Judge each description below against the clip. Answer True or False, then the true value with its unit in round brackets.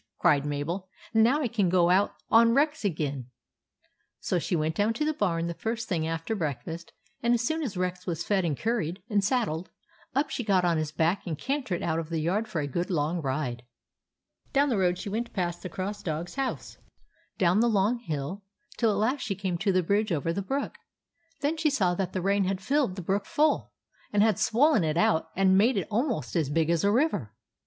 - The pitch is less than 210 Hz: True (190 Hz)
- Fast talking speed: True (225 wpm)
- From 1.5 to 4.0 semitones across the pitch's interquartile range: False (5.3 semitones)